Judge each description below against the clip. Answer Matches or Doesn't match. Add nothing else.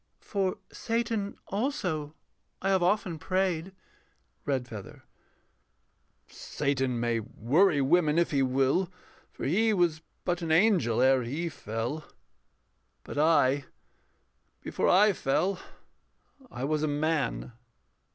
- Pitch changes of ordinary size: Doesn't match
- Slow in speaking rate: Matches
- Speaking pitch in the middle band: Matches